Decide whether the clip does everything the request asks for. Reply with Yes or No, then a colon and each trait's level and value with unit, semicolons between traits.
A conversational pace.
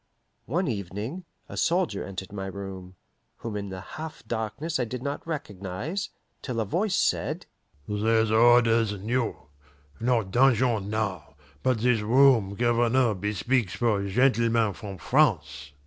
No: slow, 130 wpm